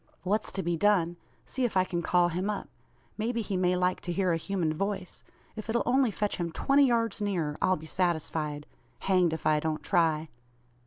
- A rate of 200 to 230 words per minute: Yes, fast, 205 wpm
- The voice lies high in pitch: No, medium, 180 Hz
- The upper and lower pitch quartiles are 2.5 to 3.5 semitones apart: No, average, 3.9 semitones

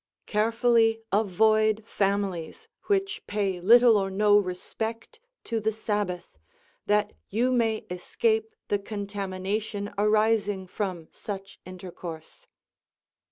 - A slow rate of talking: Yes, slow, 100 wpm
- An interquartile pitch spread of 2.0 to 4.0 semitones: Yes, narrow, 2.5 semitones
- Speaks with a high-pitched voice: Yes, high, 210 Hz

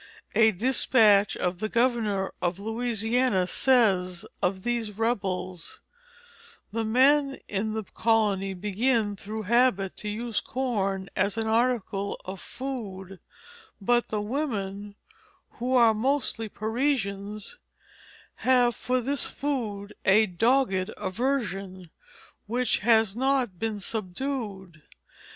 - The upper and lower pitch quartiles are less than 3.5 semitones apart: No, average, 3.9 semitones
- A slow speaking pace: Yes, slow, 110 wpm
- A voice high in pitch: Yes, high, 220 Hz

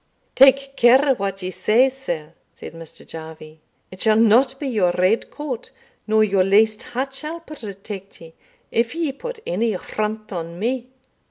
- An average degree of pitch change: No, wide, 6.1 semitones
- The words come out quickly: No, average, 160 wpm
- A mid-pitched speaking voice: No, high, 220 Hz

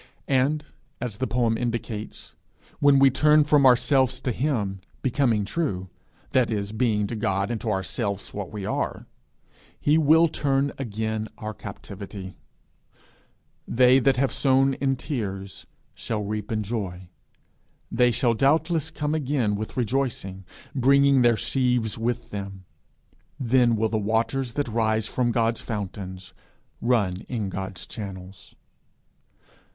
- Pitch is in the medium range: No, low, 115 Hz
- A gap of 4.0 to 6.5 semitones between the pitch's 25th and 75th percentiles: Yes, average, 4.4 semitones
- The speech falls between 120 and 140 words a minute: Yes, slow, 135 wpm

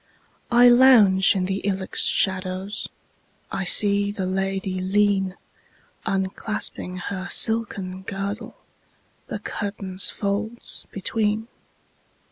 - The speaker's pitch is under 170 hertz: No, high, 195 Hz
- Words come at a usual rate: No, slow, 80 wpm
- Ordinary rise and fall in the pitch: No, narrow, 1.6 semitones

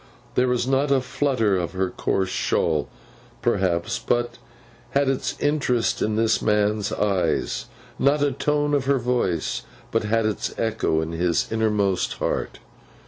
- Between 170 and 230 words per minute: No, average, 145 wpm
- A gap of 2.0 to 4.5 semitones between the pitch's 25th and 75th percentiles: No, average, 5.3 semitones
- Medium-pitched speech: No, low, 110 Hz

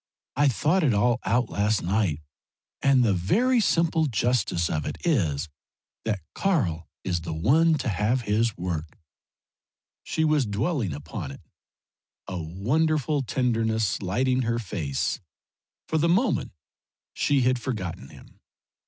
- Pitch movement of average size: No, wide, 7.8 semitones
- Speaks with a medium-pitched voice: No, low, 115 Hz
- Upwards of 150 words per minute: No, slow, 135 wpm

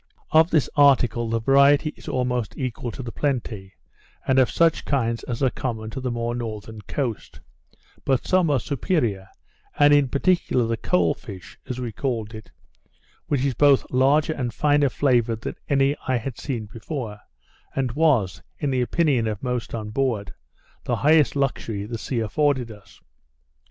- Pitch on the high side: No, low, 125 Hz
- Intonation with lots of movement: No, average, 3.9 semitones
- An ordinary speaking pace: Yes, average, 165 wpm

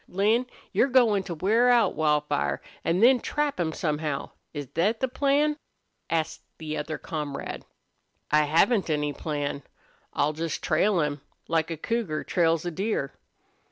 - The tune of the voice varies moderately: No, wide, 6.7 semitones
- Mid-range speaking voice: Yes, medium, 165 Hz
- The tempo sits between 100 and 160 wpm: Yes, average, 150 wpm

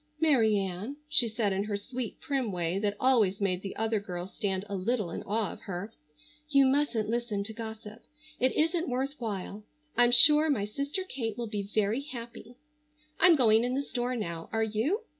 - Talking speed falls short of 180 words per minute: No, average, 190 wpm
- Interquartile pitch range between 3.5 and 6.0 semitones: Yes, average, 4.2 semitones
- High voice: Yes, high, 225 Hz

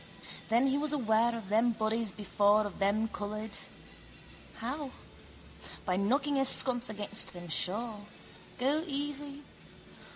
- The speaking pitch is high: Yes, high, 225 Hz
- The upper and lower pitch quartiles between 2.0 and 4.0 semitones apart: No, average, 4.6 semitones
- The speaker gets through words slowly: Yes, slow, 125 wpm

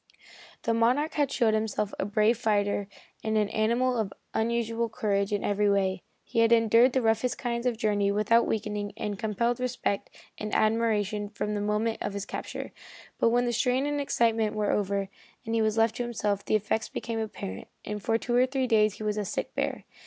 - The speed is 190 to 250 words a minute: Yes, fast, 205 wpm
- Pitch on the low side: No, high, 220 Hz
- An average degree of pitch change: No, narrow, 2.1 semitones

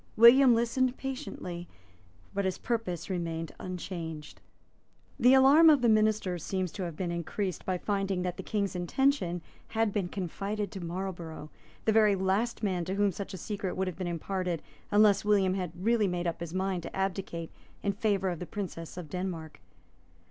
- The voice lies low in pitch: No, high, 190 Hz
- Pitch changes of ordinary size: Yes, average, 3.2 semitones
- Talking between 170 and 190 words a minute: Yes, average, 175 wpm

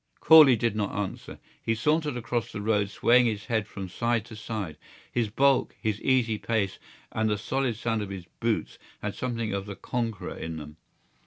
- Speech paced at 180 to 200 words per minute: Yes, average, 185 wpm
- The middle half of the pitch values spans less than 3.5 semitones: Yes, average, 2.7 semitones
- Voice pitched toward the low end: Yes, low, 110 Hz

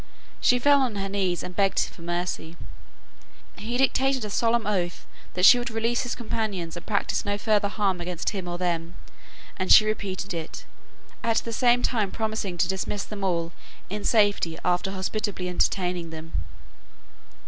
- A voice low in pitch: No, high, 200 Hz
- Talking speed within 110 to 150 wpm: No, average, 165 wpm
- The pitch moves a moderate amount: Yes, average, 3.8 semitones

